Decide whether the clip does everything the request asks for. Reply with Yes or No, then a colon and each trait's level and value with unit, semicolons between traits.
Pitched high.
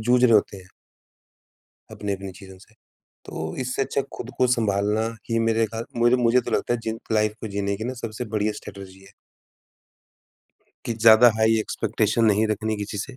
No: low, 110 Hz